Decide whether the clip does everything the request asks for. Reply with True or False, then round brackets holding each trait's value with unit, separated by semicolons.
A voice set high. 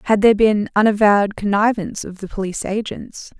True (205 Hz)